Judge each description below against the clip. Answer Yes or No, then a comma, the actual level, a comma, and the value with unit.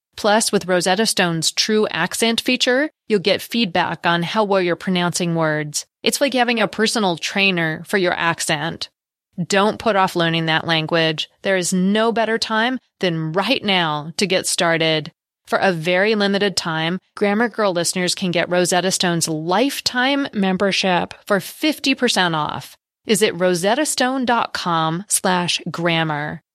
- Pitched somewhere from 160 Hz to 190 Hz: Yes, medium, 185 Hz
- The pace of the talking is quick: No, average, 145 wpm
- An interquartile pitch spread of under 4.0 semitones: No, average, 4.3 semitones